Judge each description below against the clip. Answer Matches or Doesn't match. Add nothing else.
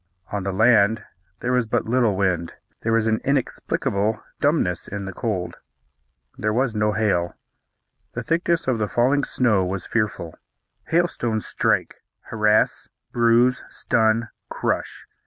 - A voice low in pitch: Matches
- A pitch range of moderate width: Matches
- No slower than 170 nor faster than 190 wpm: Doesn't match